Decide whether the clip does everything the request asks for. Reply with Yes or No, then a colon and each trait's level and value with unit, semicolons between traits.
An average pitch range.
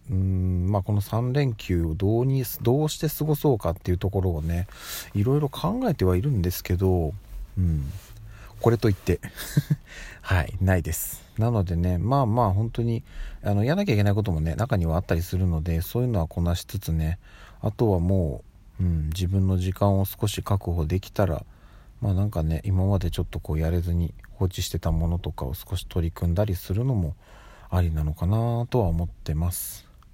Yes: average, 3.9 semitones